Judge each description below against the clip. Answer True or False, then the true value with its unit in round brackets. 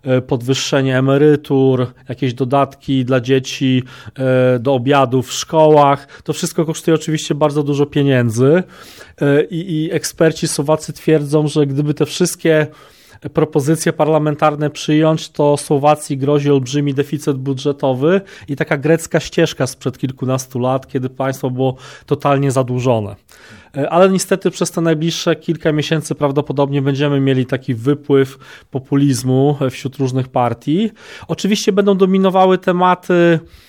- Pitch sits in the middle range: True (145 Hz)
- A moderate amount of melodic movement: True (3.0 semitones)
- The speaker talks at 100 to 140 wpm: True (120 wpm)